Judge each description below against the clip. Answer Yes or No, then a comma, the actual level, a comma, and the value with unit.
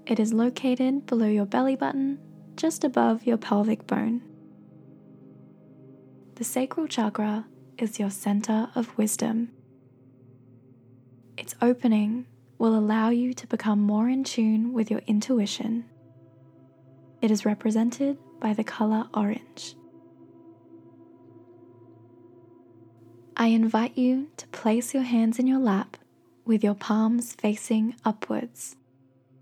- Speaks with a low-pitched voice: No, high, 215 Hz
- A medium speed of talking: No, slow, 110 wpm